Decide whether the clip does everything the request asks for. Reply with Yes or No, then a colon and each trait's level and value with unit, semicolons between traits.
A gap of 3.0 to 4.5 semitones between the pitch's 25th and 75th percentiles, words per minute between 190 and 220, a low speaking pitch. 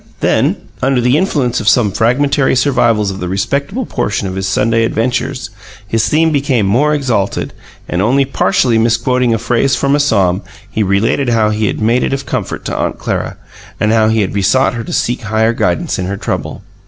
Yes: average, 3.9 semitones; average, 195 wpm; low, 115 Hz